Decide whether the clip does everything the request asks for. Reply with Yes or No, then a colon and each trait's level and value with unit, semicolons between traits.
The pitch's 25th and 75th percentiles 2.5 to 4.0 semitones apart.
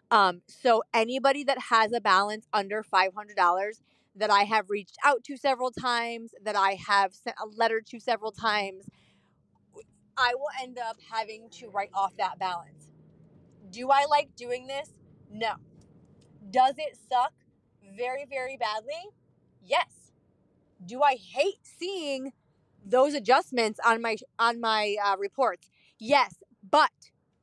No: average, 4.5 semitones